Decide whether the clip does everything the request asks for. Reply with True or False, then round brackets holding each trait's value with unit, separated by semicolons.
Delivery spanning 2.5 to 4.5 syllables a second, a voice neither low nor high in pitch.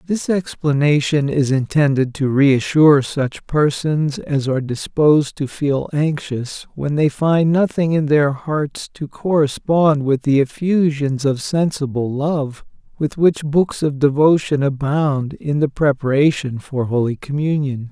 True (4.0 syllables/s; 145 Hz)